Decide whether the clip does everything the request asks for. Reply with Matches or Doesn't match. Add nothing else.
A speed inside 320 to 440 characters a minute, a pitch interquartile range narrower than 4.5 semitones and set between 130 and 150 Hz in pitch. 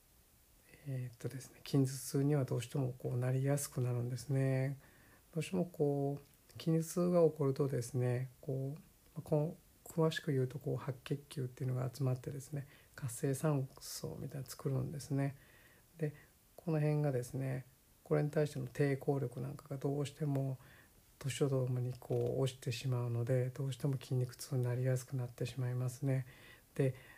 Matches